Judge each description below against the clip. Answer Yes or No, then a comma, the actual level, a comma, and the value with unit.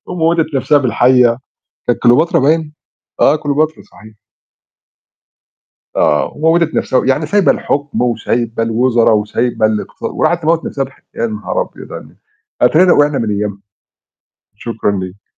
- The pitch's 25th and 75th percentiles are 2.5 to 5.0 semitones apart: No, wide, 5.4 semitones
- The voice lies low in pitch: Yes, low, 130 Hz